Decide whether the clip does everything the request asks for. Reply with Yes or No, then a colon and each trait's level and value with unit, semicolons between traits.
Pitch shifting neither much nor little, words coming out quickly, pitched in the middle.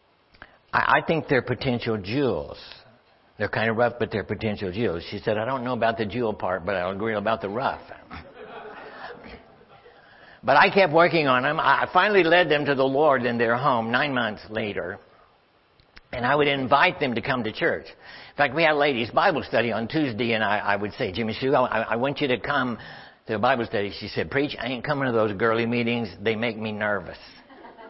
No: average, 4.3 semitones; fast, 210 wpm; low, 120 Hz